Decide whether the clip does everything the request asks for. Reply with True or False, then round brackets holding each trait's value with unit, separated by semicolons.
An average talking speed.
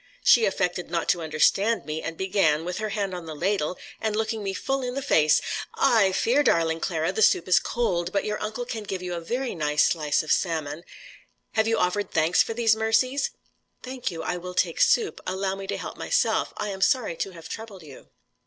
False (215 wpm)